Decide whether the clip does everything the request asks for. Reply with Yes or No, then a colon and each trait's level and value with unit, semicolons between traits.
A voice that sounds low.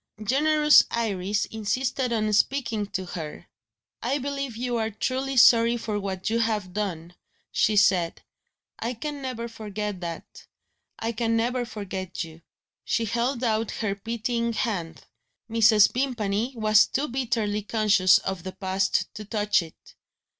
No: high, 220 Hz